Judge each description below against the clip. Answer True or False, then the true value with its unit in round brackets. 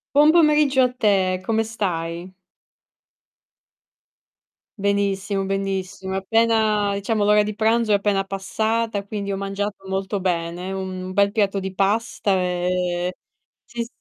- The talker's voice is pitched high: True (200 Hz)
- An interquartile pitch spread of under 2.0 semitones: False (2.4 semitones)